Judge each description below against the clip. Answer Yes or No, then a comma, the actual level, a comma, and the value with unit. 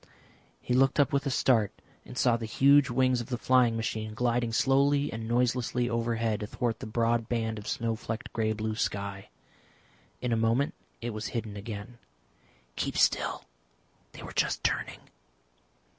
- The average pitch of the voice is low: Yes, low, 115 Hz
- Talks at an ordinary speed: Yes, average, 160 wpm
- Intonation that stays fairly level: Yes, narrow, 2.1 semitones